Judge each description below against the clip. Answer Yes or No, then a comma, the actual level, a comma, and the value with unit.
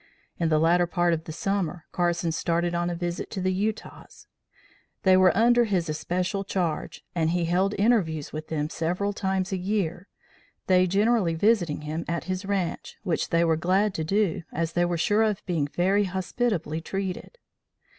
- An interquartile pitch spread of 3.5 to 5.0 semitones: No, average, 2.9 semitones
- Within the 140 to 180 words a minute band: Yes, average, 175 wpm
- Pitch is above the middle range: No, medium, 180 Hz